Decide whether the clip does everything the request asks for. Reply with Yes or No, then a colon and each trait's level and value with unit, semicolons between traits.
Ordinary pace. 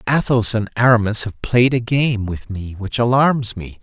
Yes: average, 190 wpm